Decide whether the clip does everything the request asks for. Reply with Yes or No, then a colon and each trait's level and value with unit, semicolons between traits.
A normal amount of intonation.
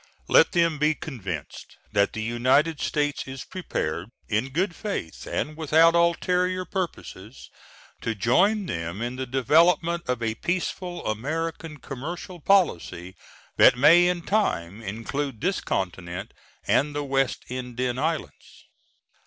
No: wide, 6.9 semitones